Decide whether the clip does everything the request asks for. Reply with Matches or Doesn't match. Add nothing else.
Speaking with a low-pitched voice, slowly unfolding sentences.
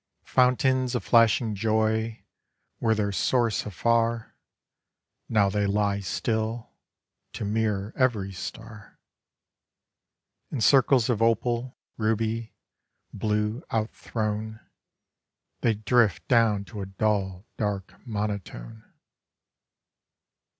Matches